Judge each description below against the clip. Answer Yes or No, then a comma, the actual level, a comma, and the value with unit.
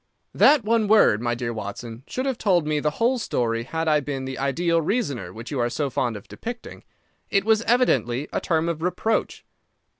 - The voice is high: No, medium, 150 Hz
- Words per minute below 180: No, average, 200 wpm